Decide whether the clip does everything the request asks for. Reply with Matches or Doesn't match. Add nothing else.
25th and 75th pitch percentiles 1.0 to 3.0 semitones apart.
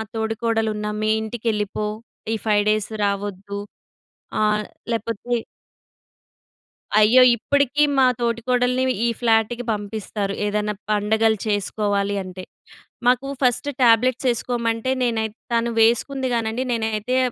Matches